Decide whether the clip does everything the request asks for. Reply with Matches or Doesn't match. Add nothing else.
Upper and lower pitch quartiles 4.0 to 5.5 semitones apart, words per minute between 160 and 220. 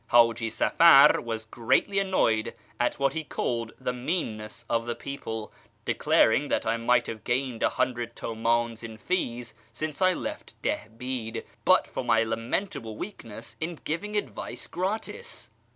Doesn't match